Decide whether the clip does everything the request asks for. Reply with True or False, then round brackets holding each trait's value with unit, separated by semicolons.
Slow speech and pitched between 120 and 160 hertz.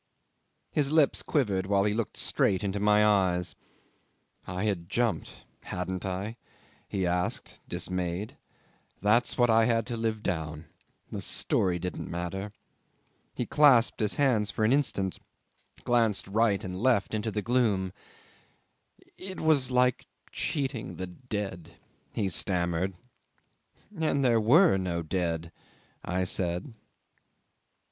False (125 wpm; 105 Hz)